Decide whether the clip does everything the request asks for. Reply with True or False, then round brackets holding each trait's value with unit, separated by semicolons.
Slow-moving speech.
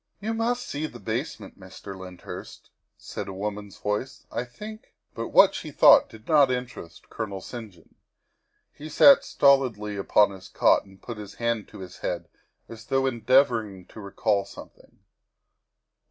False (165 wpm)